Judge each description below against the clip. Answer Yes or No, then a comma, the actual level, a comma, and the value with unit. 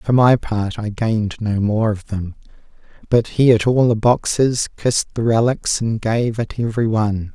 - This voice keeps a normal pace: Yes, average, 180 wpm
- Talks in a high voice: No, low, 110 Hz